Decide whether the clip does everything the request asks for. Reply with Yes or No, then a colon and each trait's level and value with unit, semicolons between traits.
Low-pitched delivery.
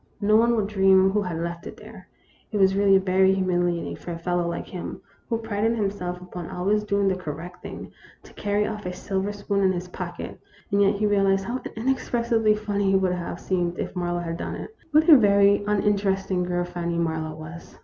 No: high, 195 Hz